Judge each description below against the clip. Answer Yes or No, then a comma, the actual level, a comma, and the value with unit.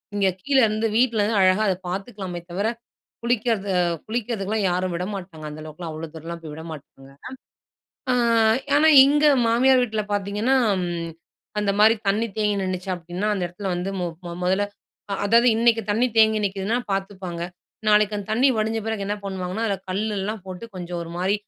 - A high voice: Yes, high, 200 Hz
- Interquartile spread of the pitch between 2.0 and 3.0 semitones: No, average, 3.4 semitones